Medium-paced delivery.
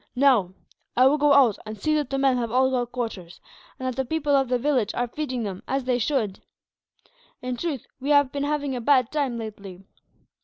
No: fast, 215 wpm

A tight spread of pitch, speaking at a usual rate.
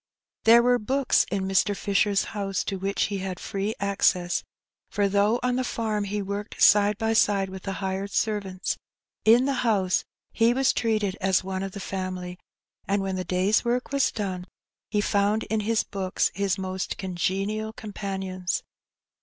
Yes: narrow, 2.3 semitones; average, 170 wpm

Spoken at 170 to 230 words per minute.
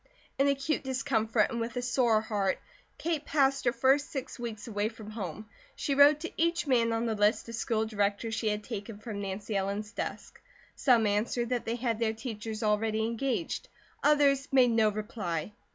Yes: average, 185 wpm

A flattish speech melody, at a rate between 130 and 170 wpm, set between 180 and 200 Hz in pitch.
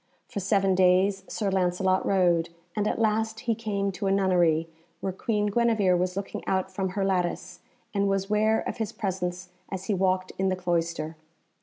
No: narrow, 2.0 semitones; average, 180 wpm; high, 190 Hz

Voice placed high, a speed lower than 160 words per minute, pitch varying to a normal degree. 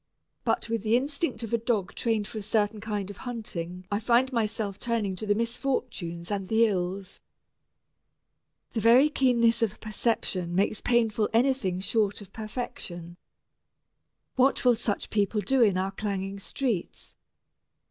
Yes: high, 215 Hz; average, 145 wpm; average, 3.1 semitones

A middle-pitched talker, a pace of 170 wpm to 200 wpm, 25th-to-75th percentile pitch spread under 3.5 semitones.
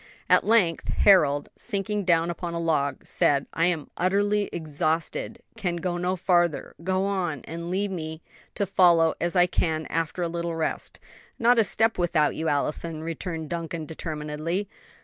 No: medium, 170 Hz; average, 160 wpm; average, 2.8 semitones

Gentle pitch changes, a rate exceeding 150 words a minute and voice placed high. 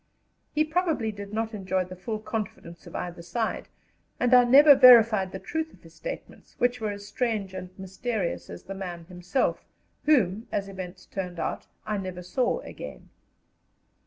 No: average, 4.8 semitones; average, 165 wpm; high, 205 Hz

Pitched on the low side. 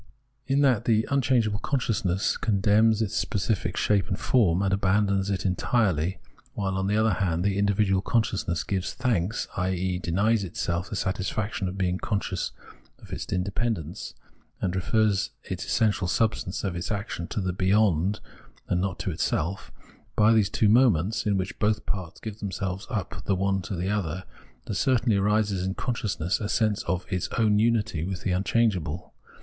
Yes: low, 100 Hz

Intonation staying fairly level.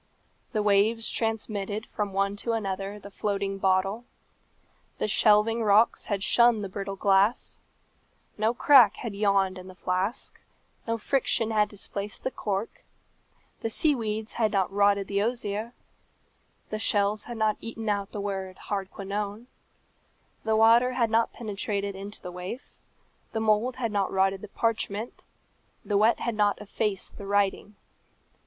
Yes: narrow, 2.1 semitones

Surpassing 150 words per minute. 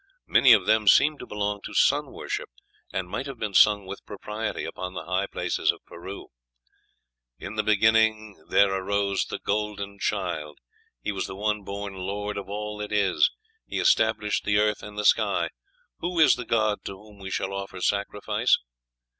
Yes: average, 180 wpm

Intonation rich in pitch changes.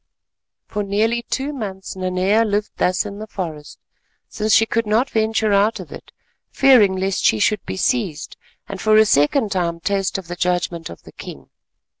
No: average, 3.1 semitones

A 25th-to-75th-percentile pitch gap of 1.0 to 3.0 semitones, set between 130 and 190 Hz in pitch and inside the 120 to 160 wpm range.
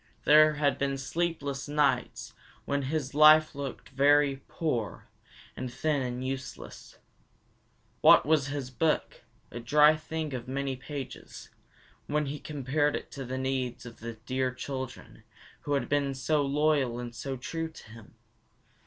Yes: narrow, 2.5 semitones; medium, 140 Hz; average, 150 wpm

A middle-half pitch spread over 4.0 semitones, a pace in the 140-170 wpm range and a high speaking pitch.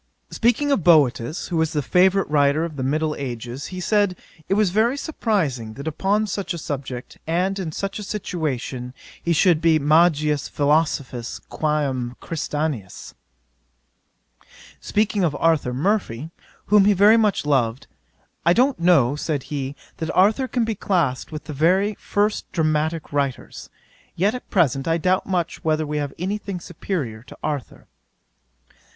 No: wide, 5.4 semitones; average, 155 wpm; medium, 160 Hz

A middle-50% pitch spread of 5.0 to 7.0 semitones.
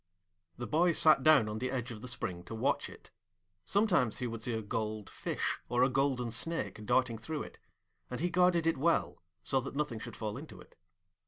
Yes: wide, 5.6 semitones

